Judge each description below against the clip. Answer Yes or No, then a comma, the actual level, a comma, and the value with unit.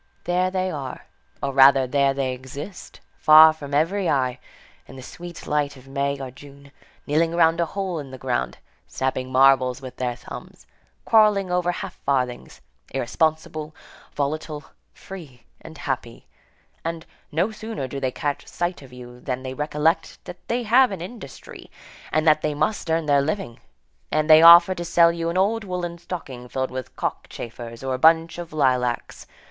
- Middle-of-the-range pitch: Yes, medium, 150 Hz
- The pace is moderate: Yes, average, 170 wpm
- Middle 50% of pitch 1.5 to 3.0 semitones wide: No, average, 4.5 semitones